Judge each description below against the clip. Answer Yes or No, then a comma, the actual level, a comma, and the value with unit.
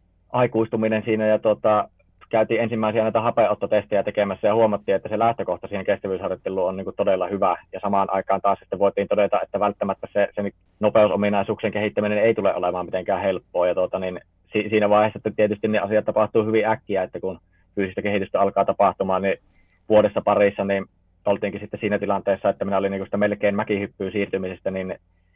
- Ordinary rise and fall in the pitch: No, narrow, 1.9 semitones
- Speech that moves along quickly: Yes, fast, 175 wpm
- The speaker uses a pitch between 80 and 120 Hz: Yes, low, 100 Hz